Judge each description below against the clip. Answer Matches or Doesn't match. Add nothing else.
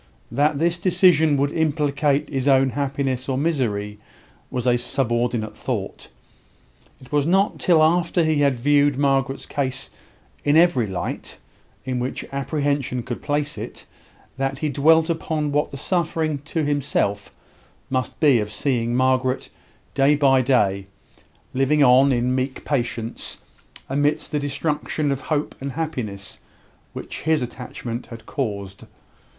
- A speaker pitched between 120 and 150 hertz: Matches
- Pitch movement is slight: Doesn't match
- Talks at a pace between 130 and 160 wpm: Matches